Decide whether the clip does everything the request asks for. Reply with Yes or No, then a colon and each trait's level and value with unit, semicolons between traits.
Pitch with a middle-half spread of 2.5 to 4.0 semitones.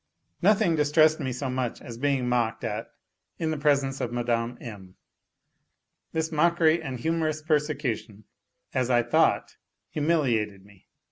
No: average, 4.8 semitones